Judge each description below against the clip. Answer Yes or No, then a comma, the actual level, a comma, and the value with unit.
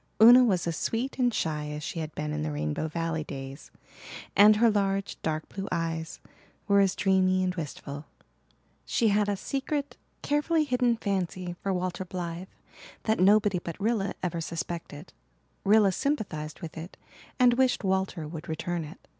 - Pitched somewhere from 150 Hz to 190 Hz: Yes, medium, 185 Hz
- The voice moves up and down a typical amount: Yes, average, 4.7 semitones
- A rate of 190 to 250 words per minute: No, average, 165 wpm